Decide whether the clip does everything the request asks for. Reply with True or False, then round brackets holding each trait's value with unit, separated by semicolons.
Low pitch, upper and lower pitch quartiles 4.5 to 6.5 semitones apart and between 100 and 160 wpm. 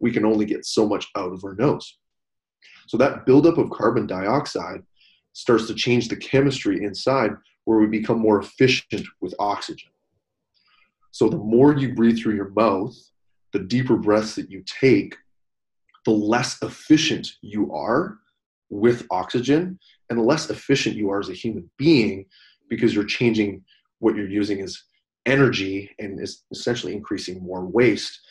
False (110 Hz; 3.3 semitones; 155 wpm)